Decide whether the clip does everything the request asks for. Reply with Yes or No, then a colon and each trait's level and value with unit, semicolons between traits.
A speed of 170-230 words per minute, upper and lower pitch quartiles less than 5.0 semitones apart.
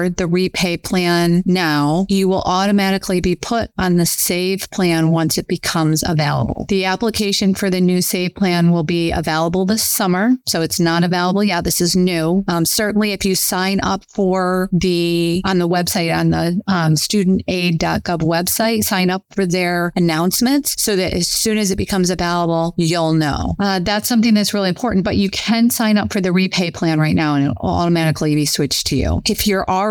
Yes: average, 190 wpm; narrow, 2.5 semitones